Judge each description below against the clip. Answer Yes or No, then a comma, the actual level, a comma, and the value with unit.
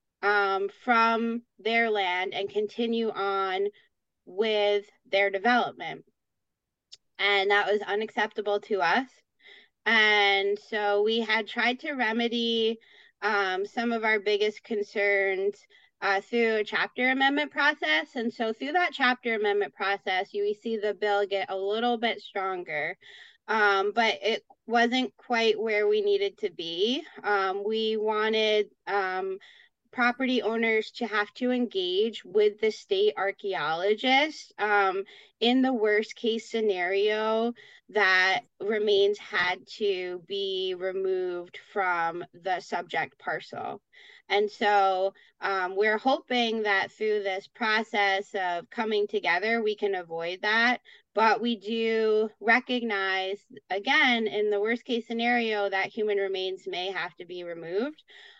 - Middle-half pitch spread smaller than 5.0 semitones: Yes, average, 3.2 semitones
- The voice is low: No, high, 215 Hz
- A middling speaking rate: No, slow, 130 wpm